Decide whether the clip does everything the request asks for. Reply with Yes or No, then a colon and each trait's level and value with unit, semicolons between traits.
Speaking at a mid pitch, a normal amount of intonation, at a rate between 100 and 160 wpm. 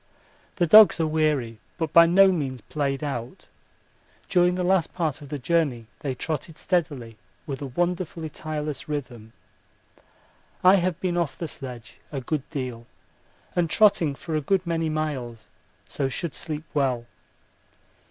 Yes: medium, 155 Hz; average, 4.2 semitones; average, 150 wpm